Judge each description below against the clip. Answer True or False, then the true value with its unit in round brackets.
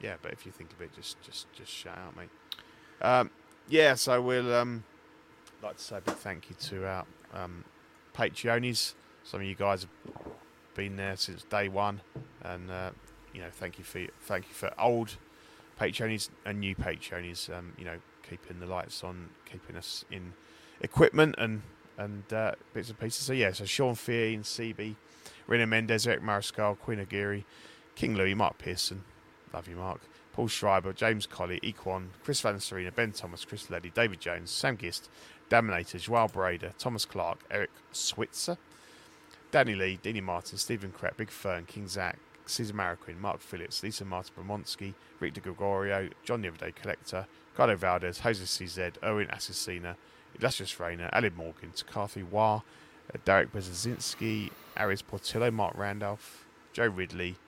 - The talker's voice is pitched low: True (100 Hz)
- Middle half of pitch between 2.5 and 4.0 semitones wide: True (3.6 semitones)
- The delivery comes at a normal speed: True (165 wpm)